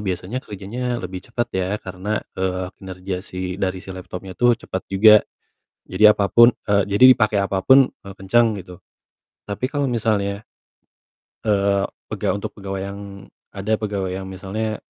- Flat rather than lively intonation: Yes, narrow, 2.3 semitones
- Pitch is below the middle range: Yes, low, 100 Hz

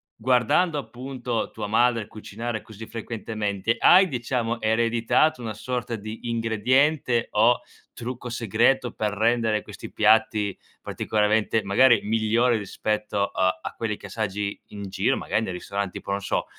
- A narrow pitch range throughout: Yes, narrow, 2.3 semitones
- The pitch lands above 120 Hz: No, low, 115 Hz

